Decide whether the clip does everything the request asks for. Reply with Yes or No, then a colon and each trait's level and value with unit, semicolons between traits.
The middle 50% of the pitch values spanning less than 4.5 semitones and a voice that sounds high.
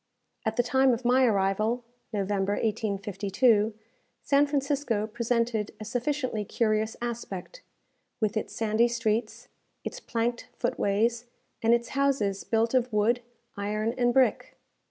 Yes: narrow, 2.6 semitones; high, 230 Hz